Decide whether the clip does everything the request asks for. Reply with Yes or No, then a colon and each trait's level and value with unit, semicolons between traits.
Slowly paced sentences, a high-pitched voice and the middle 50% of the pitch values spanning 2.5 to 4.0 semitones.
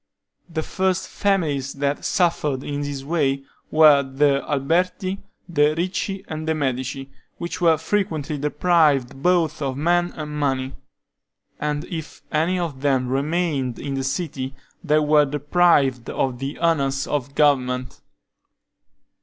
No: slow, 130 wpm; medium, 150 Hz; average, 3.5 semitones